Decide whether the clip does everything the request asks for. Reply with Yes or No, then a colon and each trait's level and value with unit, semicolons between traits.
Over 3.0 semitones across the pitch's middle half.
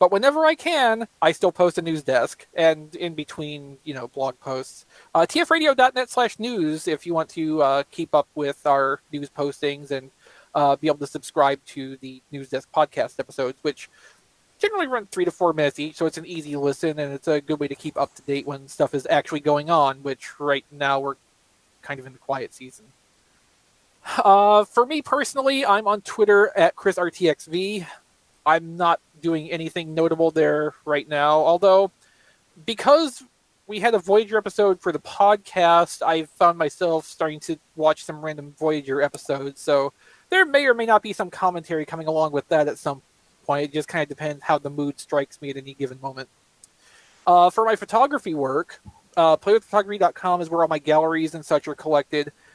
Yes: average, 5.1 semitones